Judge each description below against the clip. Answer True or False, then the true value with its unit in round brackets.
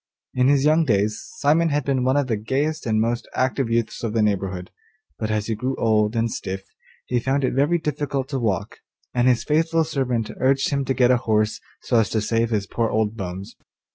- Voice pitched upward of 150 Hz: False (120 Hz)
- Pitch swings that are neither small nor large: True (4.0 semitones)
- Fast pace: True (215 wpm)